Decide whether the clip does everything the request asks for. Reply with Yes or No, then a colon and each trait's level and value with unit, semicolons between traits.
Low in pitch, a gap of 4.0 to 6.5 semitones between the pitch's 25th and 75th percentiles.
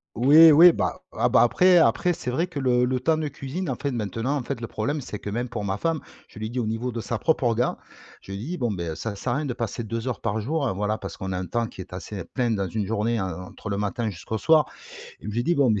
Yes: low, 120 Hz; average, 4.8 semitones